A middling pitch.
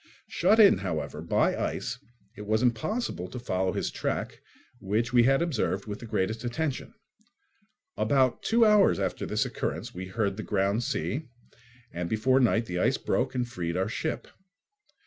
No: low, 110 Hz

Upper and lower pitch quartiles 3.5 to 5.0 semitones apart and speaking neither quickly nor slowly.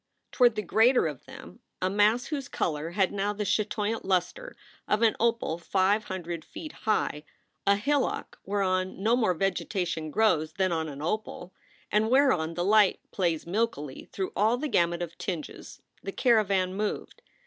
Yes: average, 4.1 semitones; average, 160 wpm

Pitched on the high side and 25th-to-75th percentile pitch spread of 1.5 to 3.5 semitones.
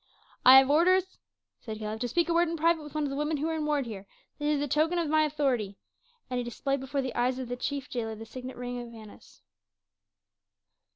No: very high, 275 Hz; average, 4.0 semitones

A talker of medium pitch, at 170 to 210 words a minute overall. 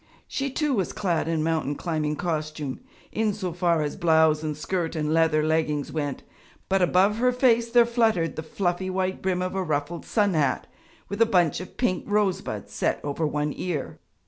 Yes: medium, 170 Hz; average, 185 wpm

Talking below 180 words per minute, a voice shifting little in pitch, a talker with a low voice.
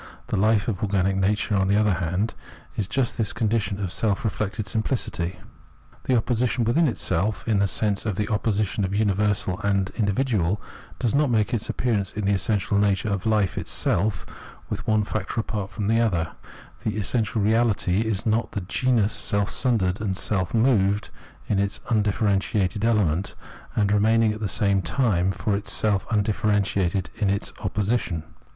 Yes: average, 165 wpm; narrow, 2.2 semitones; low, 105 Hz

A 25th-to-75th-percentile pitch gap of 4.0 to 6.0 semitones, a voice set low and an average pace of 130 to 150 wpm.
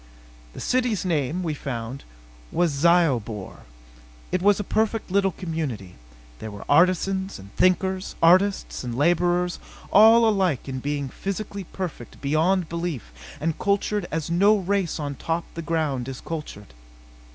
No: average, 5.2 semitones; medium, 170 Hz; average, 140 wpm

